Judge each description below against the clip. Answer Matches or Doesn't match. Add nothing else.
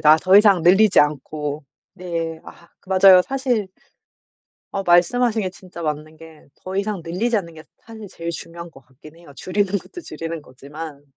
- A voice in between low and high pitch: Matches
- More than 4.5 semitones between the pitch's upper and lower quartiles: Doesn't match